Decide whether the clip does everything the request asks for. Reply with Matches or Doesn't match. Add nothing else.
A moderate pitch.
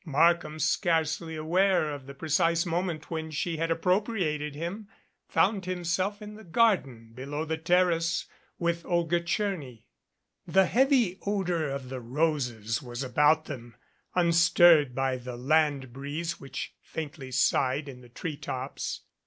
Matches